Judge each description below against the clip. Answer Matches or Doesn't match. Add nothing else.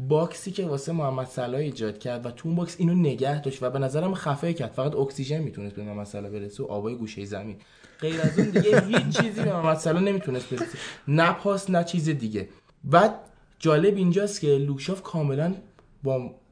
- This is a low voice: Doesn't match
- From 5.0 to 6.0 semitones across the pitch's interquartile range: Matches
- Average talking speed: Doesn't match